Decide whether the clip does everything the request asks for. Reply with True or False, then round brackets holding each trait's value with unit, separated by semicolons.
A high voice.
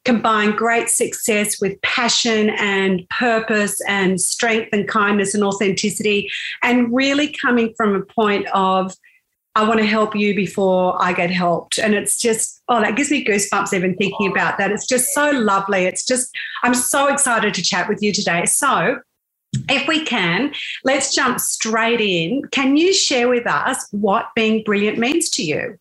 True (220 Hz)